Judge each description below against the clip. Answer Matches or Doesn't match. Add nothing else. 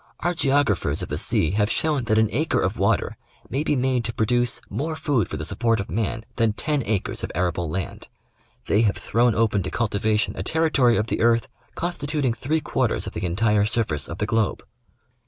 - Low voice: Matches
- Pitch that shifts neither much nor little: Matches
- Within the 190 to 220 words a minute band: Matches